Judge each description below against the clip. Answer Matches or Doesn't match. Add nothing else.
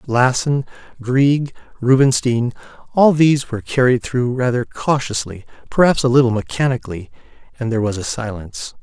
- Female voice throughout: Doesn't match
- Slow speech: Matches